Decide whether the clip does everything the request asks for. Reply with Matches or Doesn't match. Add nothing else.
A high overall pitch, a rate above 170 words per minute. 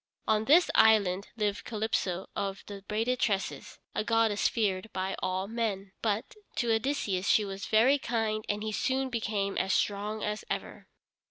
Doesn't match